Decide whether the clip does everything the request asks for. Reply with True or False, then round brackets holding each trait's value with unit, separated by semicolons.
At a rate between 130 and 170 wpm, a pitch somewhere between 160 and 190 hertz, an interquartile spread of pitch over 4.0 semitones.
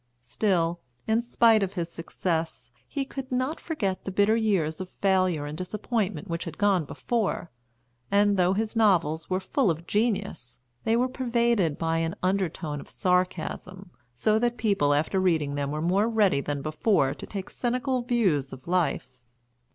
True (165 wpm; 185 Hz; 5.2 semitones)